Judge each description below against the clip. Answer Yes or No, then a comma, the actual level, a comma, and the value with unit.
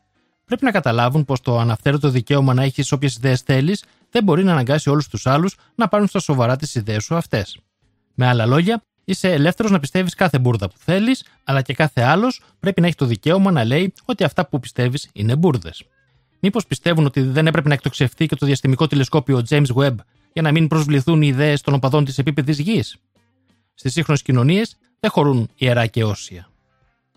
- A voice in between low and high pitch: Yes, medium, 145 Hz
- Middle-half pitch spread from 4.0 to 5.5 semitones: Yes, average, 5.2 semitones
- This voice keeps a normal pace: No, fast, 190 wpm